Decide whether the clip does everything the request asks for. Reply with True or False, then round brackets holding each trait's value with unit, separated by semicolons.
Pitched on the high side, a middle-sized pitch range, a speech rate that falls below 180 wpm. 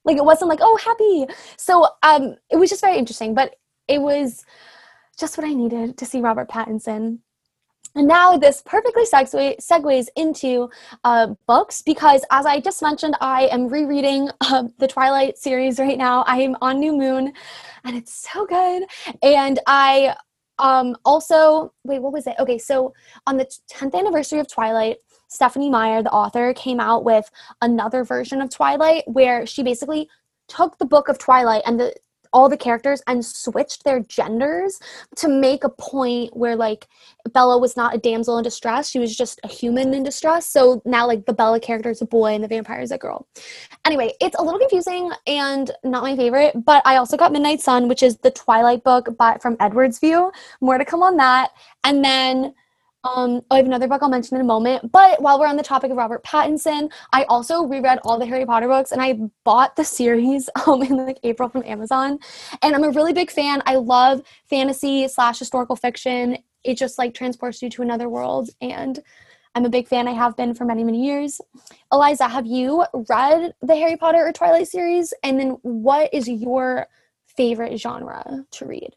False (265 Hz; 3.4 semitones; 195 wpm)